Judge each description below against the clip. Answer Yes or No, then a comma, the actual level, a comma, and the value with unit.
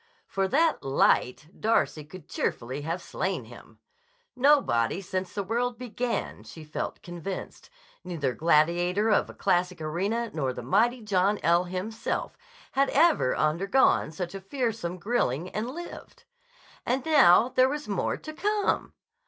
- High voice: Yes, high, 195 Hz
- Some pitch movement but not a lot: No, wide, 6.4 semitones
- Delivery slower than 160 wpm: Yes, average, 140 wpm